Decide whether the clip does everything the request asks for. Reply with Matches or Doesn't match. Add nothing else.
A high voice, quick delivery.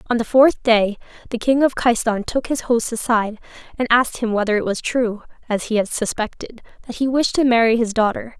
Matches